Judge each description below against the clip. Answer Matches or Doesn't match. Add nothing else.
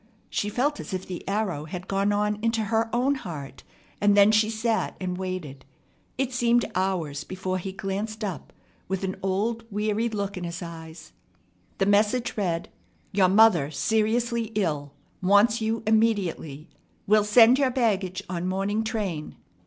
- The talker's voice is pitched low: Doesn't match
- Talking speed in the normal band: Matches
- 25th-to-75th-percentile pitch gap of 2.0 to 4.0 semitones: Matches